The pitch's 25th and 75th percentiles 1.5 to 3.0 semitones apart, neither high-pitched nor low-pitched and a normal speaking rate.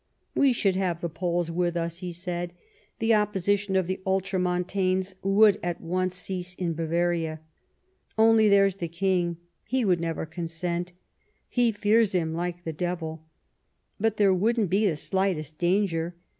Yes: narrow, 2.4 semitones; medium, 180 Hz; average, 150 wpm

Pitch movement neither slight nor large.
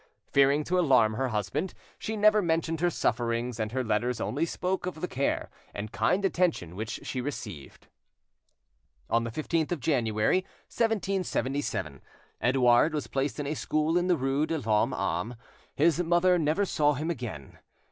No: wide, 6.4 semitones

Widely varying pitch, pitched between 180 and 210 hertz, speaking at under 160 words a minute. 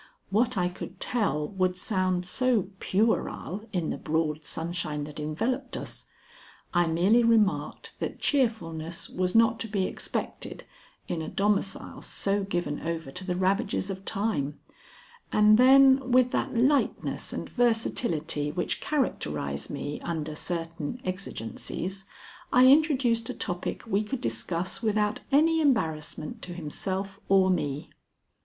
Yes: wide, 5.7 semitones; high, 190 Hz; slow, 135 wpm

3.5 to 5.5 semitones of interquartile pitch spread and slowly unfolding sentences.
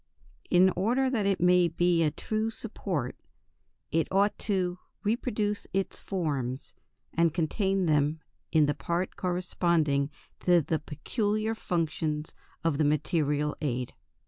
Yes: average, 4.5 semitones; slow, 125 wpm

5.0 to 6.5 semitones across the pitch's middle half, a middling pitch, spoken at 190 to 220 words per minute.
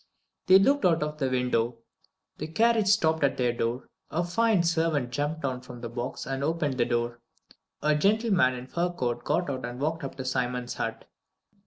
Yes: wide, 5.4 semitones; medium, 145 Hz; average, 195 wpm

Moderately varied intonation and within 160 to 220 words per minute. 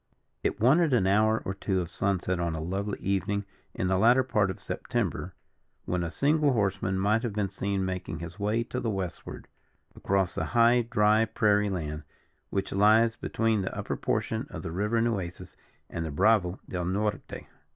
Yes: average, 3.3 semitones; average, 180 wpm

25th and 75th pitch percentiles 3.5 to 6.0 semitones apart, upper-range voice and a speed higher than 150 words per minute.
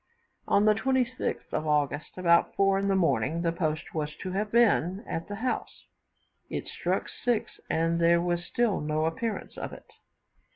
No: average, 4.3 semitones; medium, 180 Hz; average, 175 wpm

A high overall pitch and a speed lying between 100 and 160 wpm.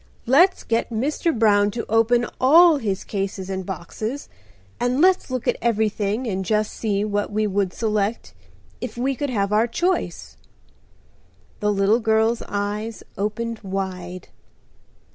Yes: high, 215 Hz; average, 140 wpm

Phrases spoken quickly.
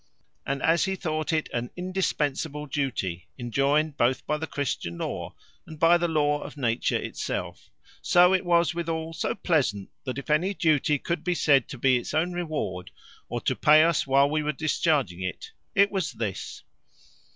No: average, 175 wpm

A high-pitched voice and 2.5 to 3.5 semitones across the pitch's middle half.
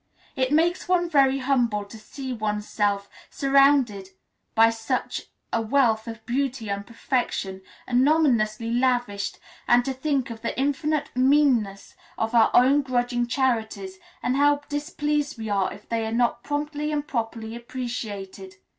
No: high, 245 Hz; average, 4.1 semitones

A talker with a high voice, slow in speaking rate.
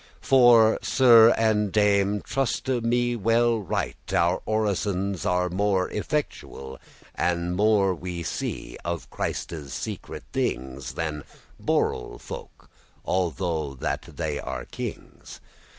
No: very low, 95 Hz; slow, 110 wpm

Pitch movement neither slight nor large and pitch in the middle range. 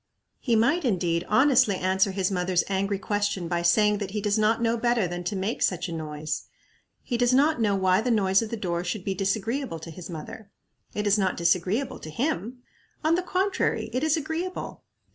No: average, 4.7 semitones; high, 205 Hz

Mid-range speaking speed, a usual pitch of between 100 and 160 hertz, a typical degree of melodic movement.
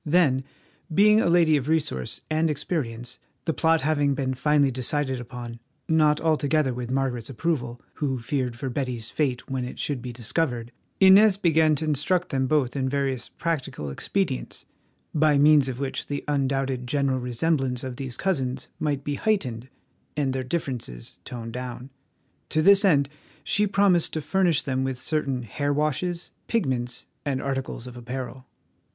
Yes: average, 160 wpm; low, 135 Hz; average, 3.7 semitones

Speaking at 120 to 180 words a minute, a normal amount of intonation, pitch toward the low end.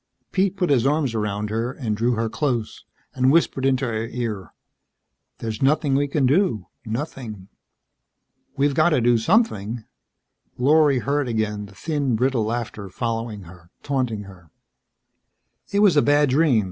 Yes: average, 150 wpm; average, 4.8 semitones; low, 125 Hz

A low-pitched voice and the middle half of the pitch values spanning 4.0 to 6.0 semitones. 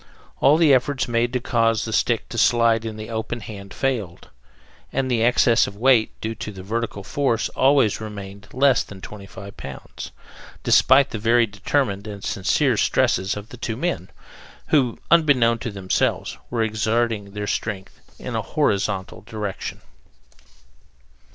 No: low, 115 Hz; average, 3.2 semitones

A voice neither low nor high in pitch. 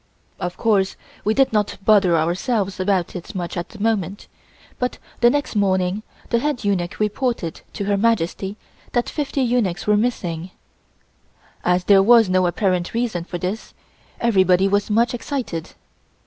No: high, 200 Hz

